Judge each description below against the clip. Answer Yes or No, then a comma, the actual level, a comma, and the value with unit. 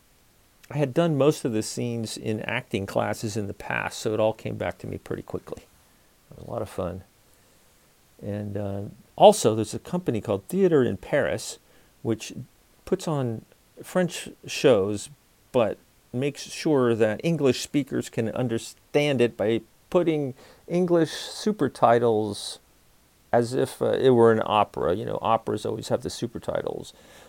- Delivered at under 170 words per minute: Yes, average, 155 wpm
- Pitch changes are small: No, average, 5.2 semitones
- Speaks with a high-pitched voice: No, low, 115 Hz